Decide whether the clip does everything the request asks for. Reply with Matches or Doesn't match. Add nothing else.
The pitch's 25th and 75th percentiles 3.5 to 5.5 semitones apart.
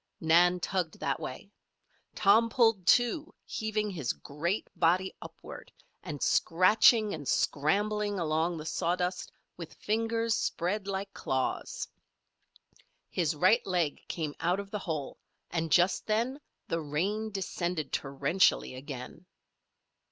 Matches